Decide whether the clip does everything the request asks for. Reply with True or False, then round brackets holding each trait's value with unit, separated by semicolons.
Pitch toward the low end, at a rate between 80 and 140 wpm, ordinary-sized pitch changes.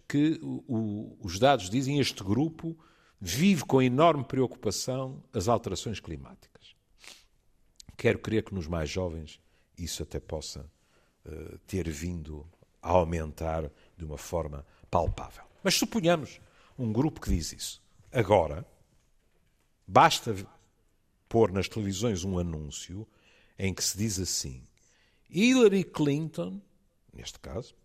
False (105 Hz; 120 wpm; 7.8 semitones)